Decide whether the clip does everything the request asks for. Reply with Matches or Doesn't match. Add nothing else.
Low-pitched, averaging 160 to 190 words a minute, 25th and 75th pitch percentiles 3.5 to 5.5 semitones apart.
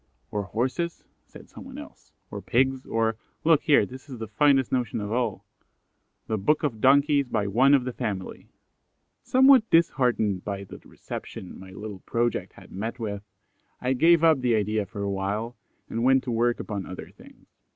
Matches